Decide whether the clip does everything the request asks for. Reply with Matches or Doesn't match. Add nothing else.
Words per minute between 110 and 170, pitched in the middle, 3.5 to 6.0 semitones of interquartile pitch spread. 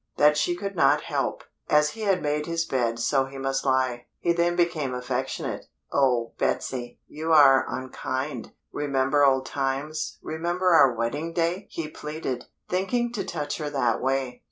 Matches